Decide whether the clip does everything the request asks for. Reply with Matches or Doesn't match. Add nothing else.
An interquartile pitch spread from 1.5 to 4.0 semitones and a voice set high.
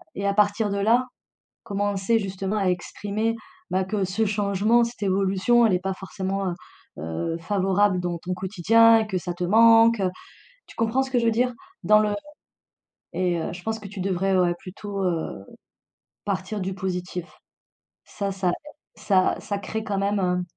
Matches